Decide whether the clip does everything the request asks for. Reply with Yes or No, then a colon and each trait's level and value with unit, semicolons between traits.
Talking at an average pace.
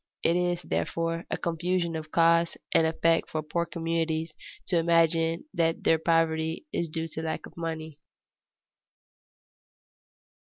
No: slow, 130 wpm